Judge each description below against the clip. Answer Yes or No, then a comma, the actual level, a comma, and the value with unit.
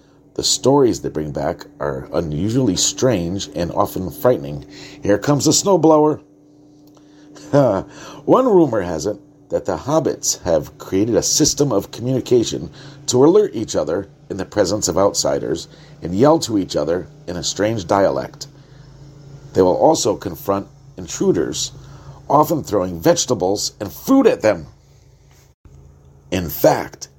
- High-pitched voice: No, medium, 140 Hz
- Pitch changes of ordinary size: No, wide, 7.4 semitones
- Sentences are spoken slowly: Yes, slow, 130 wpm